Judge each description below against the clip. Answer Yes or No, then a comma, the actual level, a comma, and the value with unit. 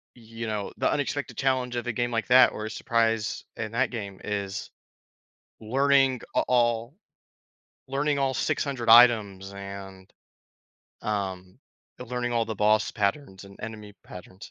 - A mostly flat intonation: No, average, 3.5 semitones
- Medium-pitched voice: No, low, 115 Hz